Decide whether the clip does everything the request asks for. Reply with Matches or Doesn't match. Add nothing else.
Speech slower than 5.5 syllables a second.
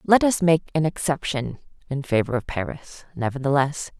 Matches